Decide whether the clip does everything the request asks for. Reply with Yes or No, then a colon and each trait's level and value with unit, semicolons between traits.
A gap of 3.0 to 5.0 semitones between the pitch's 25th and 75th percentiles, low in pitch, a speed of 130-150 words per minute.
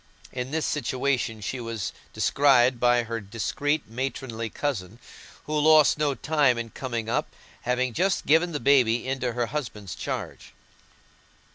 Yes: average, 4.0 semitones; low, 125 Hz; average, 140 wpm